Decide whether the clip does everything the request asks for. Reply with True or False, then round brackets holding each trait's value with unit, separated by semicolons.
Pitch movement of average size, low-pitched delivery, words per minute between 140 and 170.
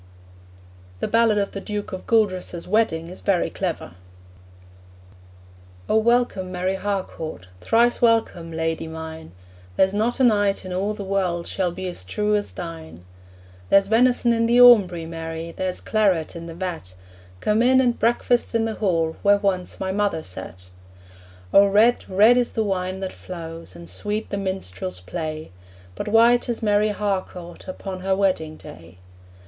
False (4.4 semitones; 190 Hz; 160 wpm)